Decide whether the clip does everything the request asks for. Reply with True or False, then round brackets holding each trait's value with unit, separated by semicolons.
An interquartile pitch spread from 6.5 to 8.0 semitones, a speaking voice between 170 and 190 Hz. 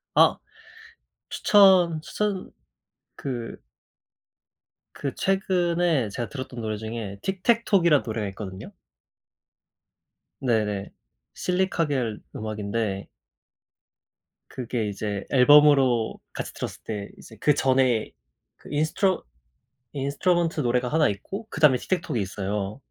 False (7.7 semitones; 130 Hz)